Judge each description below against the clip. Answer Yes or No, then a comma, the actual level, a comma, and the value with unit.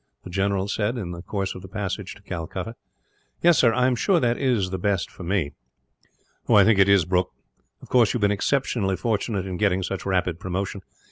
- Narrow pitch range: No, average, 3.3 semitones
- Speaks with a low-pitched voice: Yes, low, 100 Hz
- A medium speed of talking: No, fast, 210 wpm